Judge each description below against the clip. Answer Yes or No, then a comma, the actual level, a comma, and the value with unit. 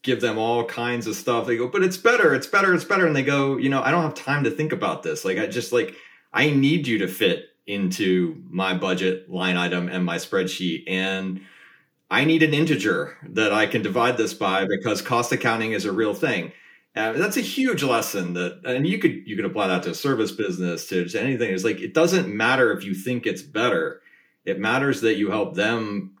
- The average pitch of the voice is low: Yes, low, 120 Hz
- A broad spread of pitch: Yes, wide, 8.7 semitones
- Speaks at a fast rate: Yes, fast, 225 wpm